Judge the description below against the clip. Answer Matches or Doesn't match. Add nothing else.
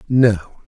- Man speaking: Matches